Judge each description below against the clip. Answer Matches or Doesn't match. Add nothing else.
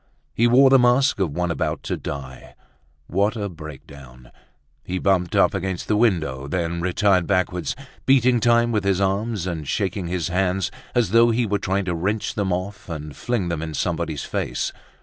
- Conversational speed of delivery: Matches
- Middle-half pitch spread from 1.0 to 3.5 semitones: Doesn't match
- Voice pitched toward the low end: Matches